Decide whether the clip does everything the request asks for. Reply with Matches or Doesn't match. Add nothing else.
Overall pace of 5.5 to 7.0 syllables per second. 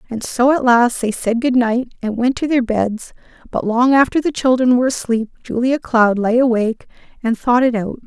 Doesn't match